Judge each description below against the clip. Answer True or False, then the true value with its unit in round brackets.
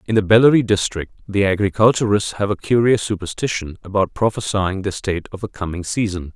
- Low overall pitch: True (100 Hz)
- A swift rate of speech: False (170 wpm)